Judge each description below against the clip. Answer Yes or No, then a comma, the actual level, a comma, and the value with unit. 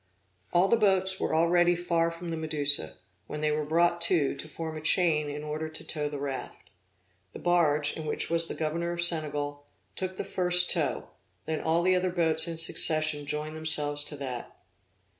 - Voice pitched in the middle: Yes, medium, 160 Hz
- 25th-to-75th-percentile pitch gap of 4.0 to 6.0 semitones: No, narrow, 2.4 semitones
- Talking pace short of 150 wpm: No, average, 190 wpm